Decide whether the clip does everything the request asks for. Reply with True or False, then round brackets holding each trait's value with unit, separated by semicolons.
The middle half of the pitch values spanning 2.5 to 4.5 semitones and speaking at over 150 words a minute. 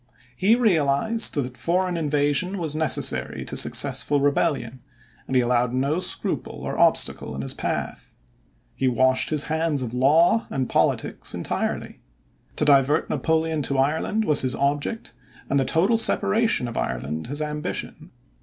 False (4.0 semitones; 145 wpm)